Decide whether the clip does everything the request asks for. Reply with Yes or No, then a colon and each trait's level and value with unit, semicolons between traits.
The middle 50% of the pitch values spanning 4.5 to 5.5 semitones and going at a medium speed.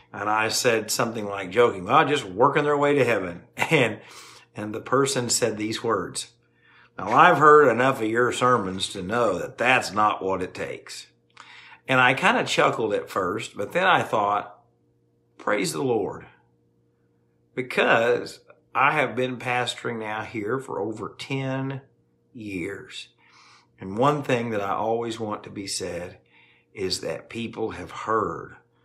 Yes: average, 4.9 semitones; average, 155 wpm